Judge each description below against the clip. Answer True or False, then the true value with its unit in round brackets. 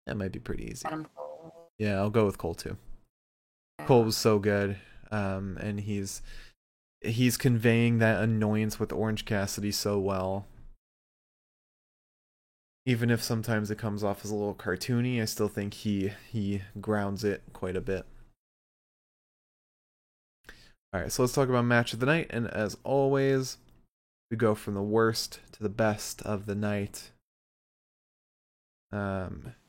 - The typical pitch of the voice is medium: False (105 Hz)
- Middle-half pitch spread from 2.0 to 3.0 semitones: True (2.7 semitones)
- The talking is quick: False (145 wpm)